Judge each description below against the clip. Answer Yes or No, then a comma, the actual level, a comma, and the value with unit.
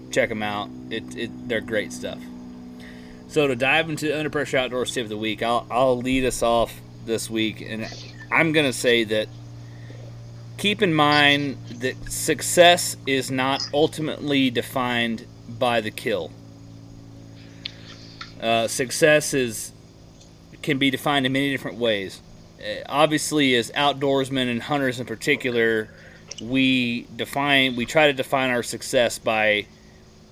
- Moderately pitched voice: No, low, 125 Hz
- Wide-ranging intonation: No, average, 3.5 semitones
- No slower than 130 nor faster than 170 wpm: Yes, average, 140 wpm